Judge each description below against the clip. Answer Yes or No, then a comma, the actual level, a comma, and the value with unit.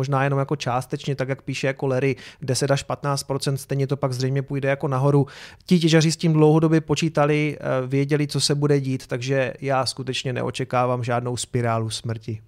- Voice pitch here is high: No, low, 135 Hz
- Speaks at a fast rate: Yes, fast, 180 wpm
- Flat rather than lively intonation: Yes, narrow, 2.1 semitones